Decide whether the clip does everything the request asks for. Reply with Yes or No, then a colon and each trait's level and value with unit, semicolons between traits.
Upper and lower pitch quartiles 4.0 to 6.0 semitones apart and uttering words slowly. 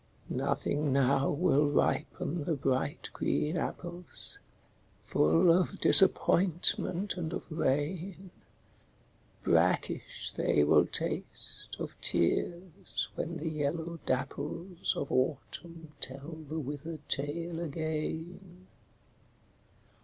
No: average, 3.4 semitones; slow, 95 wpm